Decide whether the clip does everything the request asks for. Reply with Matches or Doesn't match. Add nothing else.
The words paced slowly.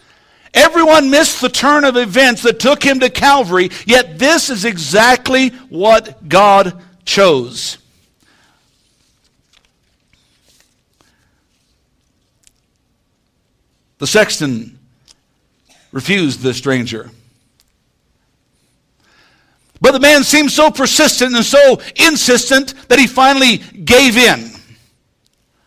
Matches